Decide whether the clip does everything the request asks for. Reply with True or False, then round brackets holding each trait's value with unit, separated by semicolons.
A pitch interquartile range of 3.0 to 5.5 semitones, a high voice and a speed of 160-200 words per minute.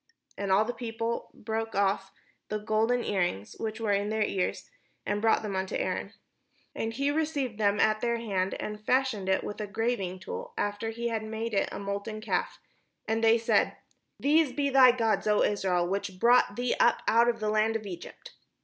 False (2.6 semitones; 220 Hz; 195 wpm)